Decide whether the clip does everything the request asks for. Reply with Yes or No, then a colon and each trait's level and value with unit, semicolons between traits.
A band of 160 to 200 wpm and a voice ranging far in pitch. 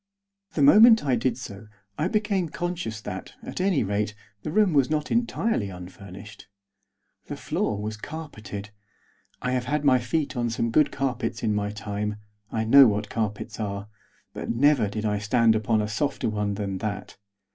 Yes: average, 170 wpm; wide, 5.8 semitones